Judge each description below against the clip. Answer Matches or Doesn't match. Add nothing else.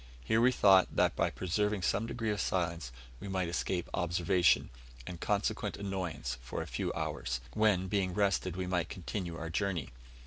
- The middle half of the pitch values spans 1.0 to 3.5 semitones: Matches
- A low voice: Matches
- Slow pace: Doesn't match